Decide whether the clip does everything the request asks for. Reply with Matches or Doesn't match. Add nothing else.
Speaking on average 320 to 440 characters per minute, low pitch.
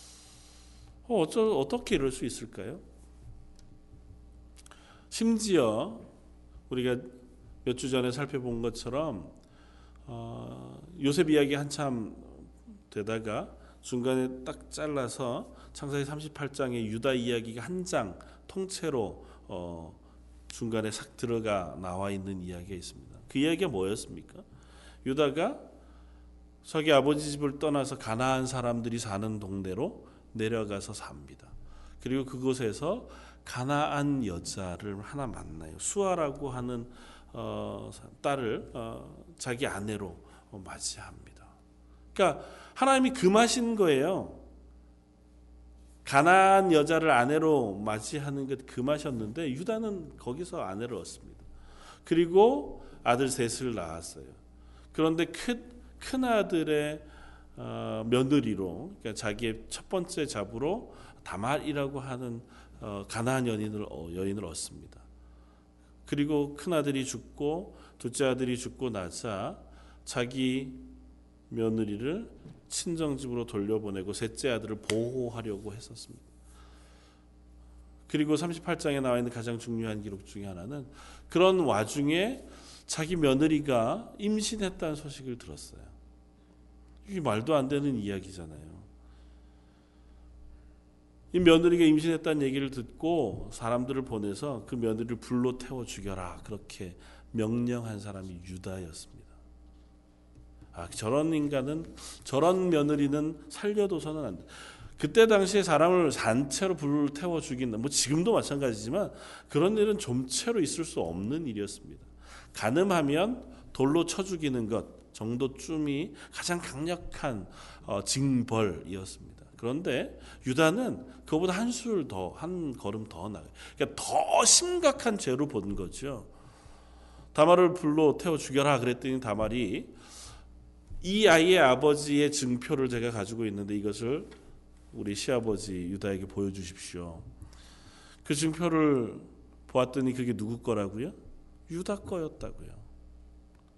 Doesn't match